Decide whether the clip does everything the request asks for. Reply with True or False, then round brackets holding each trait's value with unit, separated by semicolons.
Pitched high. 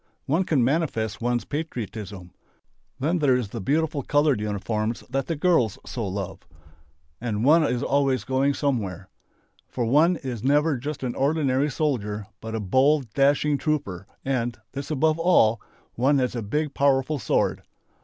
False (135 Hz)